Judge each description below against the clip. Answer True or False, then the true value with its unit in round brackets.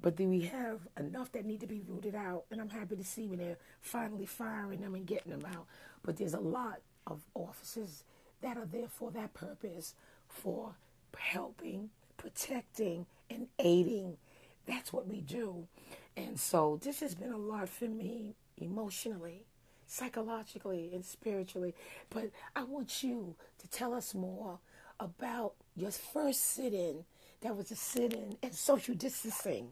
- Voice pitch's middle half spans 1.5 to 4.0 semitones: False (4.6 semitones)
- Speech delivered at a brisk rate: False (155 wpm)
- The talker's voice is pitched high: True (215 Hz)